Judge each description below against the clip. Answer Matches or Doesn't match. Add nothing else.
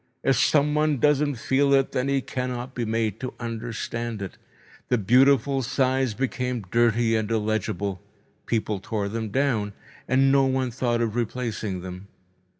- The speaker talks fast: Doesn't match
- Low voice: Matches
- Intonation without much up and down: Doesn't match